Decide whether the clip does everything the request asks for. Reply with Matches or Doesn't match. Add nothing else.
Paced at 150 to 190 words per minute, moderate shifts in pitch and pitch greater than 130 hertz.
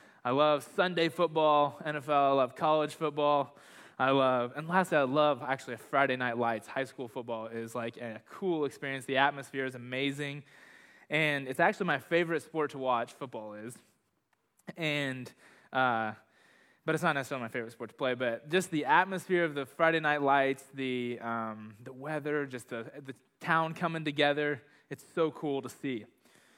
Matches